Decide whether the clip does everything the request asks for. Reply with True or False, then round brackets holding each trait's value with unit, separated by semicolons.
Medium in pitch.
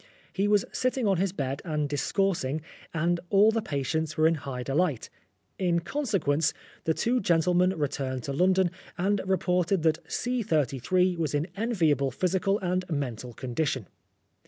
True (170 Hz)